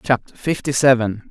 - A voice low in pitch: Yes, low, 125 Hz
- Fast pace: No, average, 140 wpm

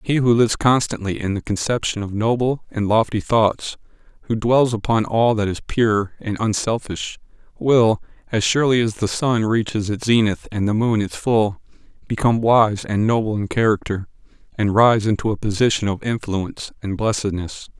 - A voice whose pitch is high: No, low, 110 Hz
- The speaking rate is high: No, average, 170 wpm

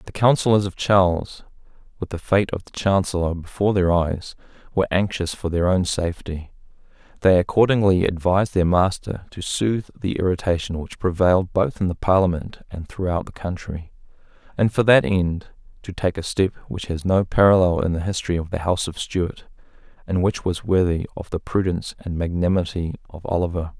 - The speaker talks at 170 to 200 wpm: Yes, average, 175 wpm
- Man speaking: Yes, male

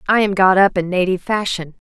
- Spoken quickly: Yes, fast, 225 wpm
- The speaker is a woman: Yes, female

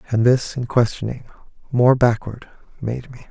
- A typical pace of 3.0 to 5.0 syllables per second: Yes, 4.7 syllables/s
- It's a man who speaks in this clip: Yes, male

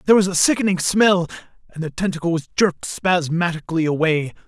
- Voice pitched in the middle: Yes, medium, 175 Hz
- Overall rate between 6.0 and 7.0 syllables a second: Yes, 6.1 syllables/s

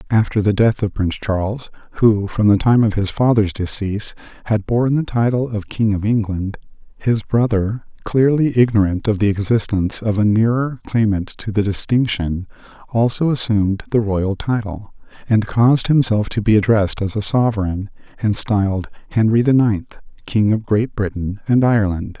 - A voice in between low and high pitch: No, low, 110 Hz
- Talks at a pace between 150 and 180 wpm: Yes, average, 165 wpm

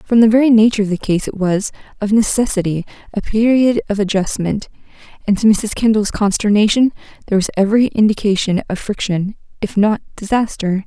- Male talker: No, female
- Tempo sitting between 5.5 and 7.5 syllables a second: Yes, 5.9 syllables/s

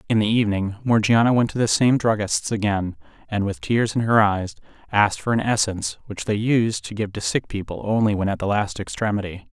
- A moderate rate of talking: No, fast, 215 wpm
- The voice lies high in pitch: No, low, 105 Hz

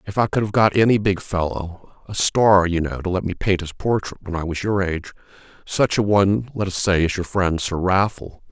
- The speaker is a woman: No, male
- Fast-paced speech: Yes, fast, 230 wpm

